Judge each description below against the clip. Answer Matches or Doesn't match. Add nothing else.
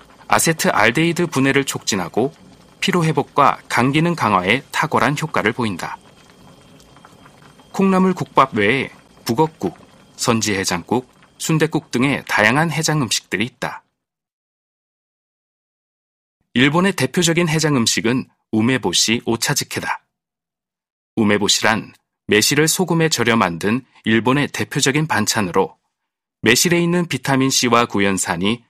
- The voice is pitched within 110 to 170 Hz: Matches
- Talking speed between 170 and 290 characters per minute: Matches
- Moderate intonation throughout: Doesn't match